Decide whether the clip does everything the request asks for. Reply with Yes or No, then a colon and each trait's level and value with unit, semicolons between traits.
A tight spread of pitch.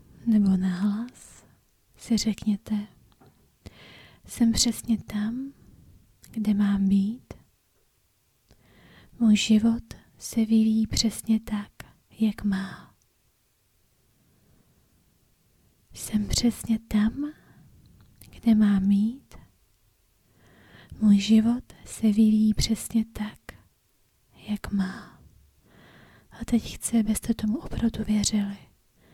Yes: narrow, 2.0 semitones